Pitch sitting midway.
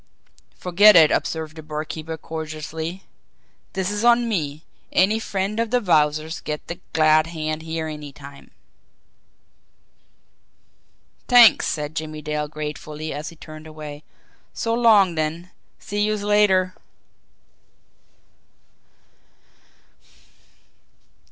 Yes: medium, 160 Hz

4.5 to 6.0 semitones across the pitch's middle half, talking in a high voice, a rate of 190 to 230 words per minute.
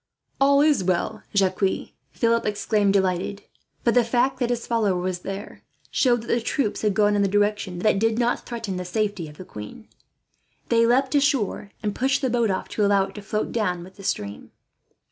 No: average, 3.7 semitones; high, 210 Hz; average, 200 wpm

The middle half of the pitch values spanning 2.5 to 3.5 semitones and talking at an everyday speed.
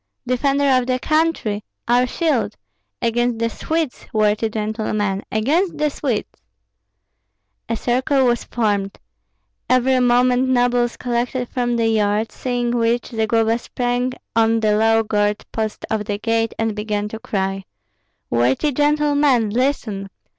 No: average, 2.8 semitones; slow, 130 wpm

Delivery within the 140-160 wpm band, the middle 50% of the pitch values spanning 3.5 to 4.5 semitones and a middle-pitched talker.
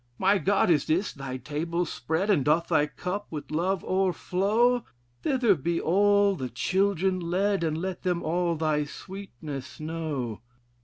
Yes: average, 150 wpm; average, 4.0 semitones; medium, 170 Hz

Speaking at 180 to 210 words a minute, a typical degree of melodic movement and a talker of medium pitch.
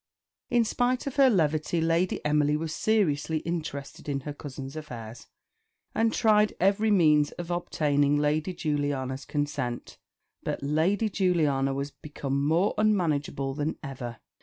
No: slow, 135 wpm; average, 4.3 semitones; medium, 150 Hz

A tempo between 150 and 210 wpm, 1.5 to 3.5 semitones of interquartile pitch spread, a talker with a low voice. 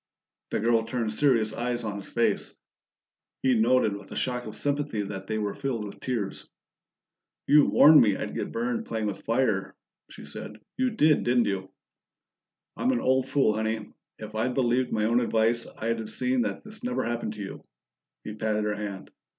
Yes: average, 185 wpm; average, 3.1 semitones; low, 115 Hz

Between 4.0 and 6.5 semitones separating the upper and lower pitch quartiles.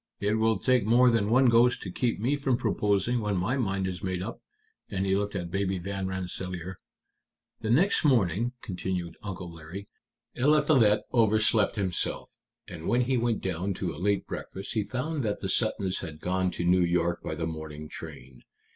Yes: average, 4.4 semitones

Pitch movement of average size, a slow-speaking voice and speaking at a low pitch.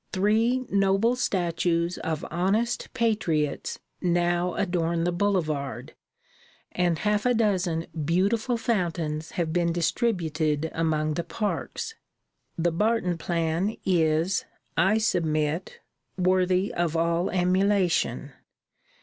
No: average, 3.5 semitones; slow, 100 wpm; medium, 175 Hz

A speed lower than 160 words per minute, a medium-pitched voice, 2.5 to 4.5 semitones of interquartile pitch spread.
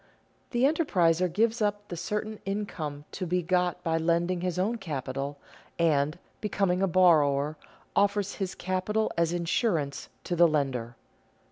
Yes: average, 140 wpm; medium, 175 Hz; average, 4.1 semitones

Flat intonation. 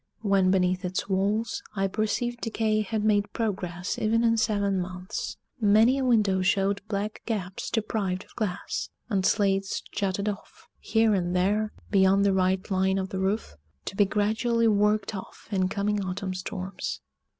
Yes: narrow, 2.3 semitones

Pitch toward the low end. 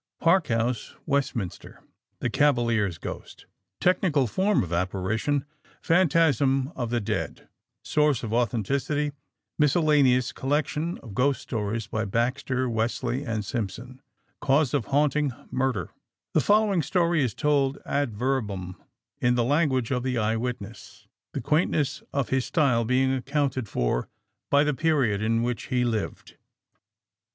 Yes: low, 130 Hz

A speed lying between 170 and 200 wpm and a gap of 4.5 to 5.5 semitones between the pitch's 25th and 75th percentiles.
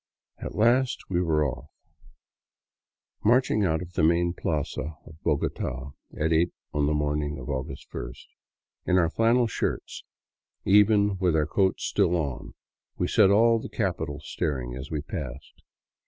No: average, 150 wpm; average, 5.2 semitones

